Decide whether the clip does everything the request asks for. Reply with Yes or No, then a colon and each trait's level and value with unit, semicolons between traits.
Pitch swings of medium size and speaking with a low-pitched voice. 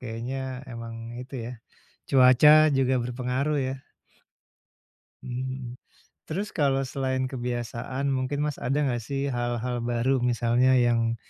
No: narrow, 2.0 semitones; low, 125 Hz